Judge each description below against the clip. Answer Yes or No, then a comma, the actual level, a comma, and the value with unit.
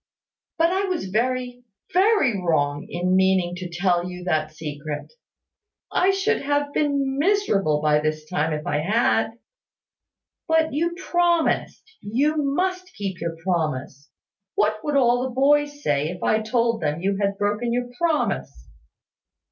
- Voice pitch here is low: No, high, 220 Hz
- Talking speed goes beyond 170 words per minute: No, average, 145 wpm